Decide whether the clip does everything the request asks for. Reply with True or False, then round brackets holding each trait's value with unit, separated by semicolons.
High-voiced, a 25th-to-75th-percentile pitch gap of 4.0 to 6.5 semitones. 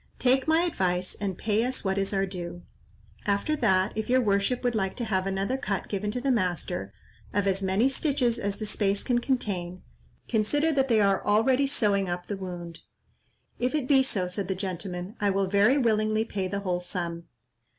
True (200 Hz; 4.5 semitones)